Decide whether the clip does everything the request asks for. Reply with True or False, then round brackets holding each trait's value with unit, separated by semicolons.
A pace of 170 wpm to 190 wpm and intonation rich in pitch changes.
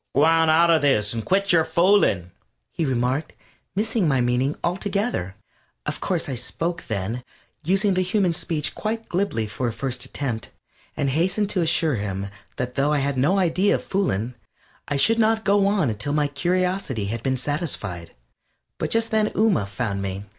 True (175 wpm; 7.4 semitones)